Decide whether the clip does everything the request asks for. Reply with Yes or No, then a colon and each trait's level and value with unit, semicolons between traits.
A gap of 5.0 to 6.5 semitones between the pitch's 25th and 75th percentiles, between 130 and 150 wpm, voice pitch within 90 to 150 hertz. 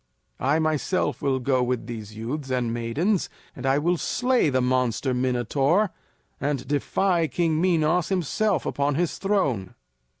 Yes: average, 5.3 semitones; average, 140 wpm; medium, 140 Hz